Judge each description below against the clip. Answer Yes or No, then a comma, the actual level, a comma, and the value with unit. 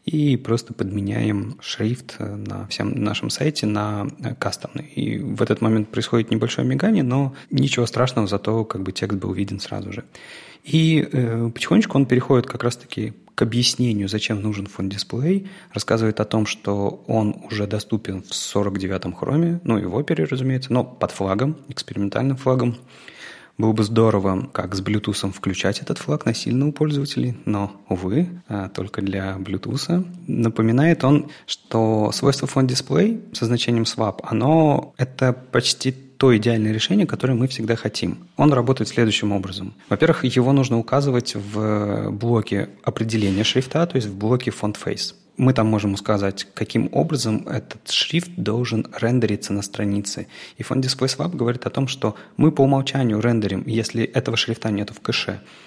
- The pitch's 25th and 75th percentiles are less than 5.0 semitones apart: Yes, average, 4.1 semitones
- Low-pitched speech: Yes, low, 115 Hz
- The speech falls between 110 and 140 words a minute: No, average, 155 wpm